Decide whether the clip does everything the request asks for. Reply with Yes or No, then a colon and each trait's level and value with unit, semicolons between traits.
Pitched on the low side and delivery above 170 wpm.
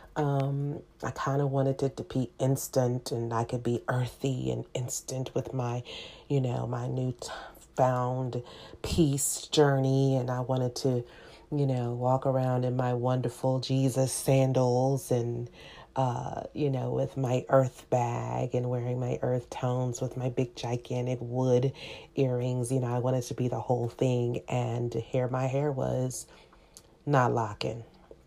No: low, 125 Hz; average, 155 wpm